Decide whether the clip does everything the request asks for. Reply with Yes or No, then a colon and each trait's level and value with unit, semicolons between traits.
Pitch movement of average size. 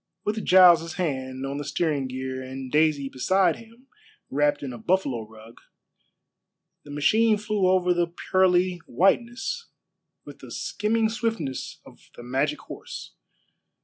No: wide, 6.6 semitones